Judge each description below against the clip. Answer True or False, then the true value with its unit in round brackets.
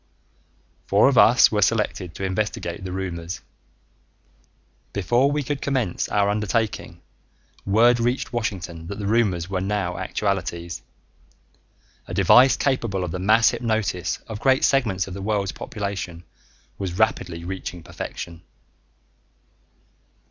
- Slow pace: True (125 wpm)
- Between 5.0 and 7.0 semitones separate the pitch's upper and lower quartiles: False (4.0 semitones)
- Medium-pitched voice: False (100 Hz)